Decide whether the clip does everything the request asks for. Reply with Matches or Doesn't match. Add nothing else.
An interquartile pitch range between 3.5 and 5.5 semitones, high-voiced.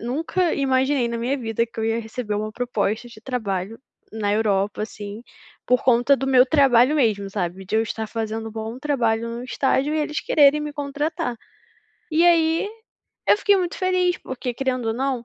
Matches